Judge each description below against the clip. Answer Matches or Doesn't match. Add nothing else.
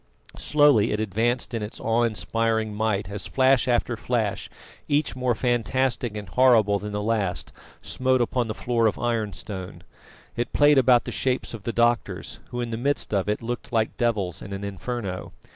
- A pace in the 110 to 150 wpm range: Doesn't match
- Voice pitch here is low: Matches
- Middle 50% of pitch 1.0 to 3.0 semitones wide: Matches